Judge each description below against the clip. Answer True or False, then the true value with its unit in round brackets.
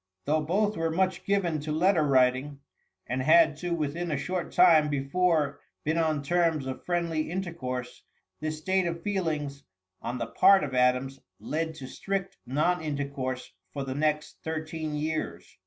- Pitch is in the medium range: True (155 Hz)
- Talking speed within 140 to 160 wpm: True (155 wpm)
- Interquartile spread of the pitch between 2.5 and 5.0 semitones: True (3.6 semitones)